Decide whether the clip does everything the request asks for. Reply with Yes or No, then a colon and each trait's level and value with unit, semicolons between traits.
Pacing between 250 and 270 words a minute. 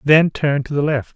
Yes: fast, 260 wpm